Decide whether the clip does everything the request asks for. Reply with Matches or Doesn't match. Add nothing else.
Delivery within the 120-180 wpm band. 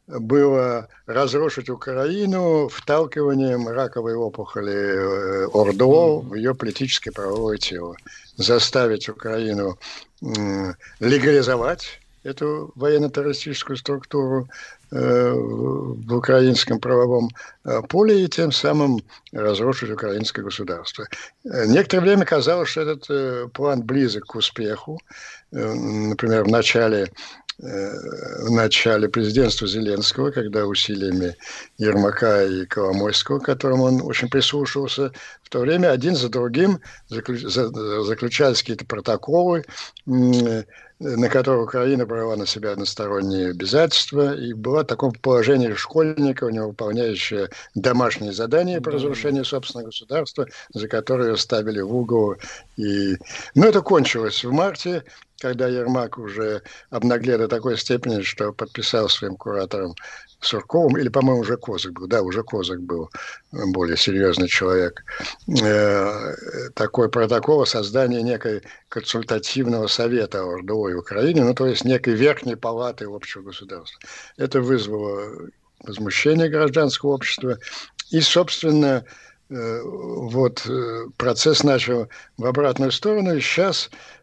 Doesn't match